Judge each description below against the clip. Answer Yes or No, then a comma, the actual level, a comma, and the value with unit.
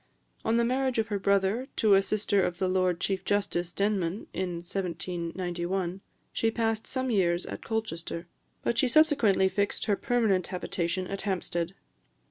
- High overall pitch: Yes, high, 195 Hz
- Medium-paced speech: Yes, average, 155 wpm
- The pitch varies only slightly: No, average, 3.7 semitones